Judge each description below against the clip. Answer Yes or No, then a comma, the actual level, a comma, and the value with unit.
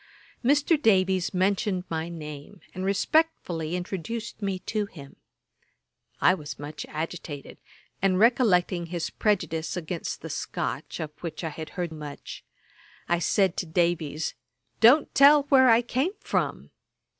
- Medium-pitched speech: Yes, medium, 180 Hz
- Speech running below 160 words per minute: Yes, slow, 135 wpm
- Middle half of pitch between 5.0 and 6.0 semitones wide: Yes, average, 5.3 semitones